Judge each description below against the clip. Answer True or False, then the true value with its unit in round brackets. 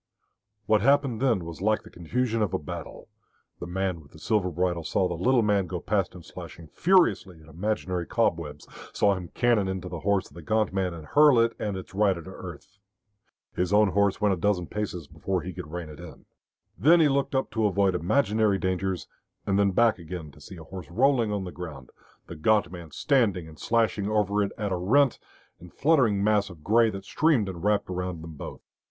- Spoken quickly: True (210 wpm)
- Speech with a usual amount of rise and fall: True (3.7 semitones)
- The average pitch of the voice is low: True (95 Hz)